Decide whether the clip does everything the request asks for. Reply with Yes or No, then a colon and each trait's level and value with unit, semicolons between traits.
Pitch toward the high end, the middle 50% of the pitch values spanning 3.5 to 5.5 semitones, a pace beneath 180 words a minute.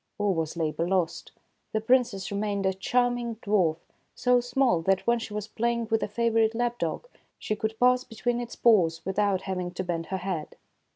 No: high, 210 Hz; average, 4.2 semitones; average, 195 wpm